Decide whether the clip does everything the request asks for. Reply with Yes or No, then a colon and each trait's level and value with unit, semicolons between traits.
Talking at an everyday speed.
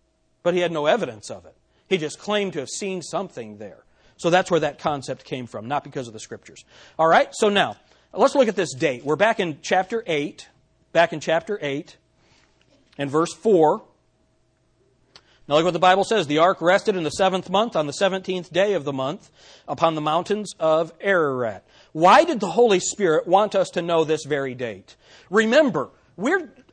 Yes: average, 195 wpm